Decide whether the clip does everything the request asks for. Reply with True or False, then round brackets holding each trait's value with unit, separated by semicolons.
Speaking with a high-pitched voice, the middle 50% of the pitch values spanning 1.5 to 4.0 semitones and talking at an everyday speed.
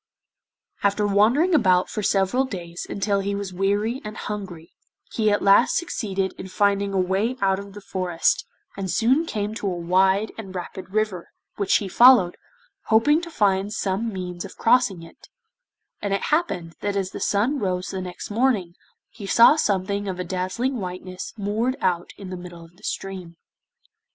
True (200 Hz; 2.6 semitones; 175 wpm)